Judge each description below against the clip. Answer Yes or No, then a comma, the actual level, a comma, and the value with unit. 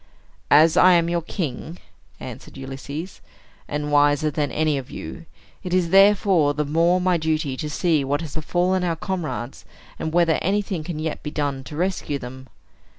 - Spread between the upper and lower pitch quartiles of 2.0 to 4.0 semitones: Yes, average, 3.3 semitones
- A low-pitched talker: No, medium, 155 Hz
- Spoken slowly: No, average, 170 wpm